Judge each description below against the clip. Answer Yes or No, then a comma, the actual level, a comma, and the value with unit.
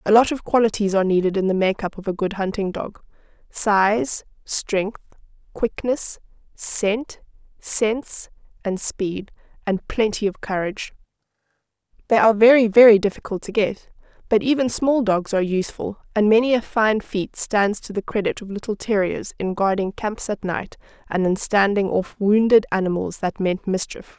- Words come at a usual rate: Yes, average, 155 wpm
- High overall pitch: Yes, high, 205 Hz